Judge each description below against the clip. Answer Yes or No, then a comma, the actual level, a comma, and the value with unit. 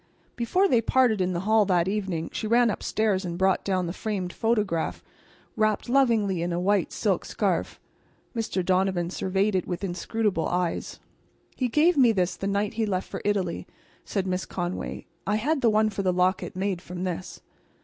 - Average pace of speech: Yes, average, 180 wpm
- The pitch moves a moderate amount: Yes, average, 3.3 semitones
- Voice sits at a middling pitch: No, high, 195 Hz